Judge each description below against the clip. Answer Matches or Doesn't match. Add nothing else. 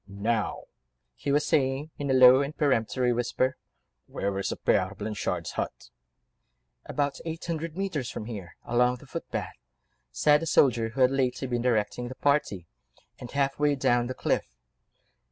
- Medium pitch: Doesn't match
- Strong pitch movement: Doesn't match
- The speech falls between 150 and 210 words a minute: Matches